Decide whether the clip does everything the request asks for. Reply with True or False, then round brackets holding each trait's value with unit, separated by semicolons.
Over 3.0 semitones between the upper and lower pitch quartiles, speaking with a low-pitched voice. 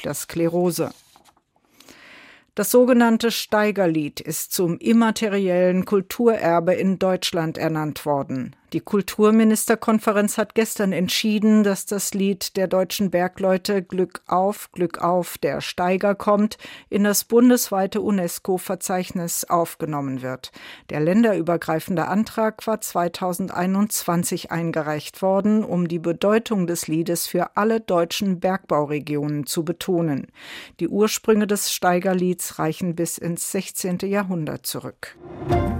False (3.4 semitones; 185 Hz)